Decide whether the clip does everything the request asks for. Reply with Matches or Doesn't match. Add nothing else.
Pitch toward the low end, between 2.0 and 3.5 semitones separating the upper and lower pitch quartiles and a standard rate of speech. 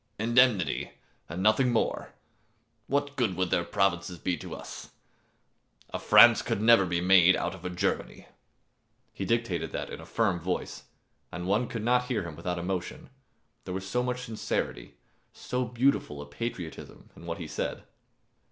Doesn't match